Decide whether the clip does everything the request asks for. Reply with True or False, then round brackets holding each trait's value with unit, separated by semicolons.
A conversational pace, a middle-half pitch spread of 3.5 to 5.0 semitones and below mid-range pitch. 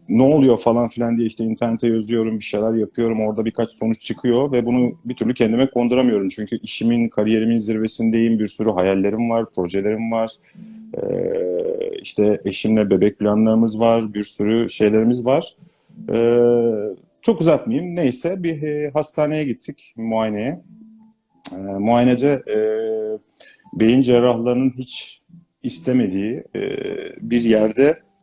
True (130 wpm; 4.1 semitones; 115 Hz)